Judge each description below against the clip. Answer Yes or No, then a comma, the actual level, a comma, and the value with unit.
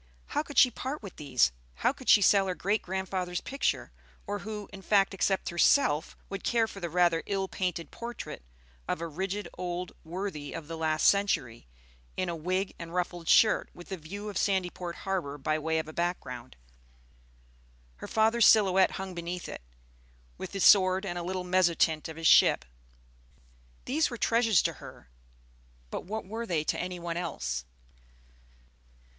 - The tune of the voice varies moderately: Yes, average, 3.3 semitones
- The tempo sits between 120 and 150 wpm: No, average, 170 wpm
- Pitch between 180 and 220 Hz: Yes, medium, 185 Hz